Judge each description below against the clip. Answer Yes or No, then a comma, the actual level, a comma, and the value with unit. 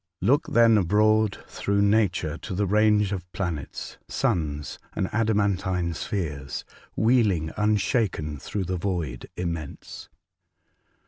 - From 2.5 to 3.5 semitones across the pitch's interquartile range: No, average, 4.1 semitones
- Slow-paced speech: Yes, slow, 110 wpm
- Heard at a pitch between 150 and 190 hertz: No, very low, 95 Hz